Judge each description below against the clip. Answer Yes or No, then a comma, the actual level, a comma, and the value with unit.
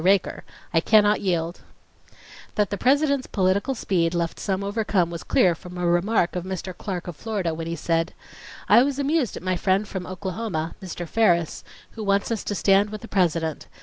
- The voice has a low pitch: No, high, 190 Hz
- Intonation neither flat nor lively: Yes, average, 3.5 semitones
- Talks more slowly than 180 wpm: No, average, 185 wpm